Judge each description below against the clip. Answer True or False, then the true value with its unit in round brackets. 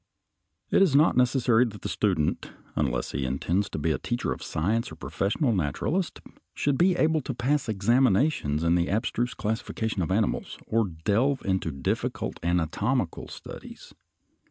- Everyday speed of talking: True (155 wpm)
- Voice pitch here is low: True (110 Hz)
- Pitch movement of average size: False (6.9 semitones)